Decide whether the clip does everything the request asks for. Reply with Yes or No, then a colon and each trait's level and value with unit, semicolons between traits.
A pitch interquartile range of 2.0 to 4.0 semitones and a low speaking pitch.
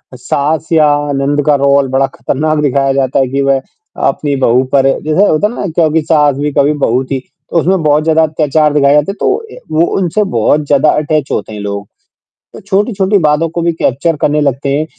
No: average, 2.7 semitones; medium, 150 Hz